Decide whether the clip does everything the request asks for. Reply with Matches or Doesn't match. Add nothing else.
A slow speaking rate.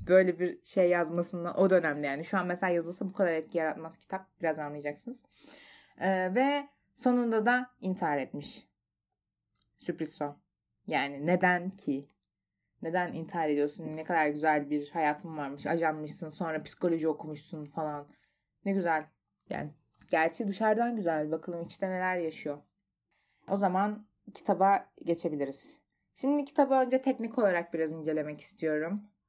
Doesn't match